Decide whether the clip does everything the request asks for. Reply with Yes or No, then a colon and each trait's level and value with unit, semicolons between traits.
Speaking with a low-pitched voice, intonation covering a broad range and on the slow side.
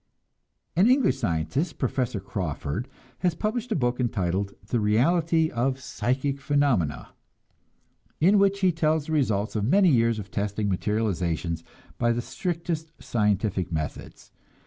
Yes: low, 120 Hz; wide, 7.8 semitones; slow, 130 wpm